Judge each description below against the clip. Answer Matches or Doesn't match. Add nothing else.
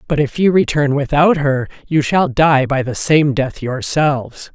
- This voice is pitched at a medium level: Matches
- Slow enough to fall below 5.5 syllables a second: Matches